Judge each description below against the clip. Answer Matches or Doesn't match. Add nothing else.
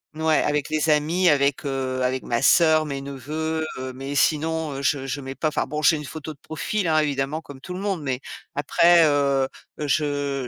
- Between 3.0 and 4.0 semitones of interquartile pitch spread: Doesn't match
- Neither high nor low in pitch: Matches